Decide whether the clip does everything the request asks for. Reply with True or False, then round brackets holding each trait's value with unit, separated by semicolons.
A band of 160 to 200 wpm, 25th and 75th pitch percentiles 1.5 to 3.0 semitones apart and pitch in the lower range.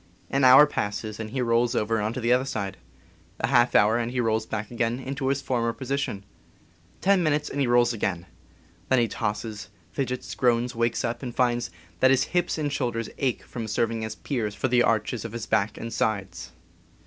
True (195 wpm; 2.7 semitones; 120 Hz)